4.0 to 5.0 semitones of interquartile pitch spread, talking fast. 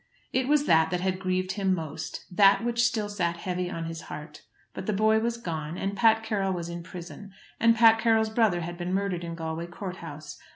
Yes: average, 4.4 semitones; fast, 215 wpm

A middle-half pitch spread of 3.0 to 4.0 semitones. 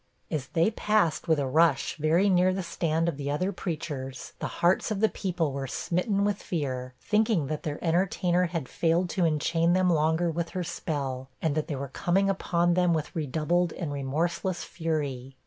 Yes: average, 3.4 semitones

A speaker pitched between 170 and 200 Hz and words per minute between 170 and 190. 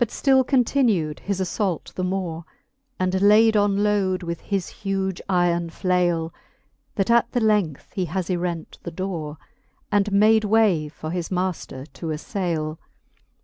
No: medium, 185 Hz; average, 145 wpm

